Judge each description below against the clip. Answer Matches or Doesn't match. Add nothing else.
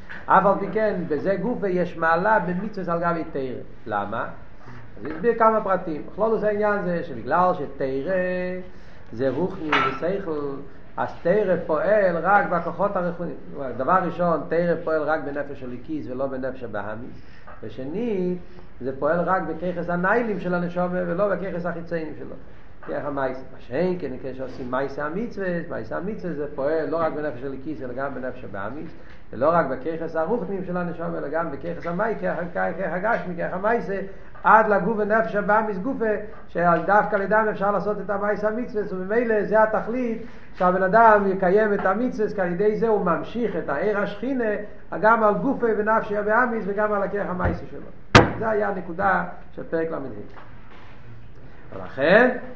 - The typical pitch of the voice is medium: Matches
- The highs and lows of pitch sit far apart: Matches